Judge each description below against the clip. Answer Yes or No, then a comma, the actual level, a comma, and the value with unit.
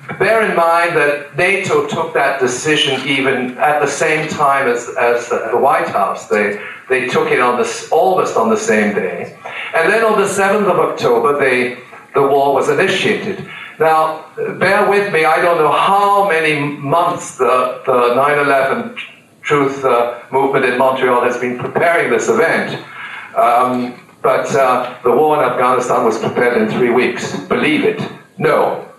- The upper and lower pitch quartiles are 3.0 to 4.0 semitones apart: No, average, 5.0 semitones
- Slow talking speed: No, average, 165 wpm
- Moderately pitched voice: Yes, medium, 145 Hz